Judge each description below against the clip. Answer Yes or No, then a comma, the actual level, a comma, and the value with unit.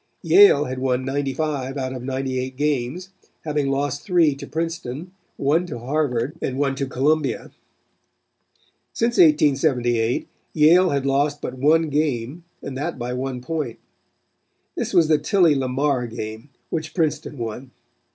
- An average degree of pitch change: Yes, average, 3.2 semitones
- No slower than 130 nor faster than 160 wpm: Yes, average, 140 wpm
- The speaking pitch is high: No, medium, 140 Hz